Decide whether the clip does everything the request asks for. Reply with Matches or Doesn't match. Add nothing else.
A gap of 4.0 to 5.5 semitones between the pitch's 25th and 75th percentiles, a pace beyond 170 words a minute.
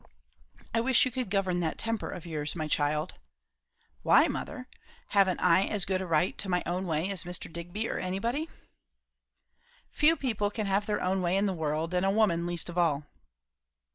Doesn't match